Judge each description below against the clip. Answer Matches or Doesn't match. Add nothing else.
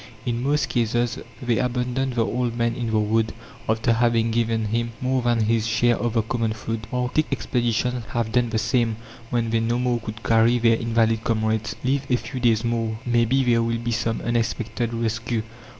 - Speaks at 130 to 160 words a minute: Doesn't match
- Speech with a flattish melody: Matches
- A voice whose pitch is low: Matches